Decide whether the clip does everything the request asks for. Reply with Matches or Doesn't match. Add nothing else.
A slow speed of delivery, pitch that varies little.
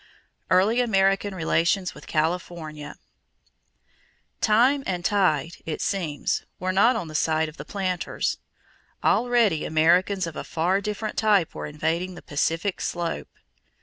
Doesn't match